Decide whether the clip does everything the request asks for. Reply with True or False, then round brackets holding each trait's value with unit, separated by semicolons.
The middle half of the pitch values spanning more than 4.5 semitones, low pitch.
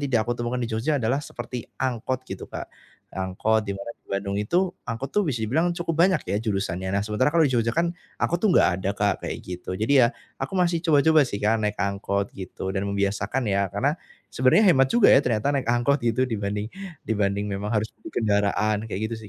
True (5.1 semitones; 110 Hz)